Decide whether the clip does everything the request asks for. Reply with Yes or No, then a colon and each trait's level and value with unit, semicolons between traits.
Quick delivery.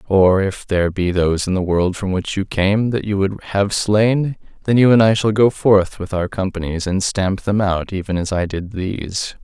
Yes: fast, 220 wpm